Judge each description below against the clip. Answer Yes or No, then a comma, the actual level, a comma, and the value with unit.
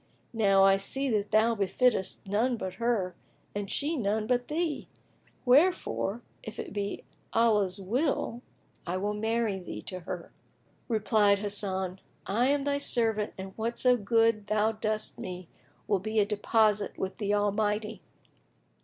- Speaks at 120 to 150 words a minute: Yes, average, 145 wpm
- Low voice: No, high, 215 Hz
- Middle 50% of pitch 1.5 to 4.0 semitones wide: Yes, average, 2.8 semitones